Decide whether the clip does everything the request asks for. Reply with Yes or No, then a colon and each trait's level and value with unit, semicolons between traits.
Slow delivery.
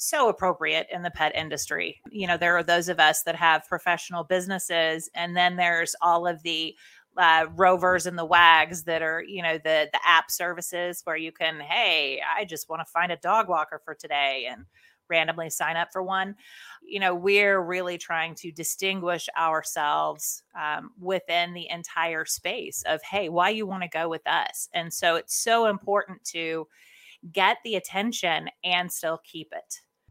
No: average, 180 wpm